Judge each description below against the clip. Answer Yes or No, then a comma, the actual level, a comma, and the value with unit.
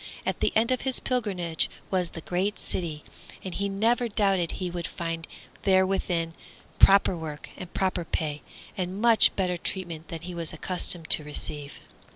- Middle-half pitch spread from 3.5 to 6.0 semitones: No, average, 2.9 semitones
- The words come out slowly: No, average, 165 wpm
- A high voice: No, medium, 180 Hz